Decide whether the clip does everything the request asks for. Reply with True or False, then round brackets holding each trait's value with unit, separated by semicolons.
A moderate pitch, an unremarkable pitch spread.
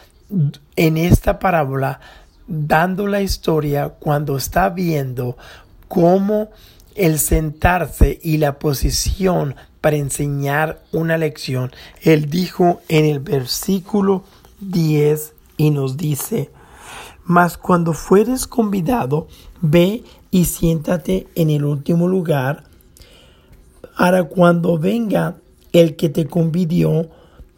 True (165 Hz; 3.4 semitones)